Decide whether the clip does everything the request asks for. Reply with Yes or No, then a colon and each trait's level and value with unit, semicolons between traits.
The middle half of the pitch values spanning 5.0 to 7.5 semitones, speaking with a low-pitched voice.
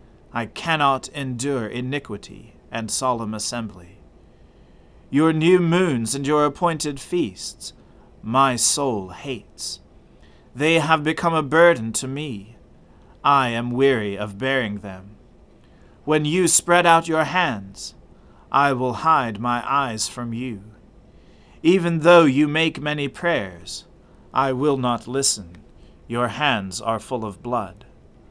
Yes: wide, 5.6 semitones; low, 125 Hz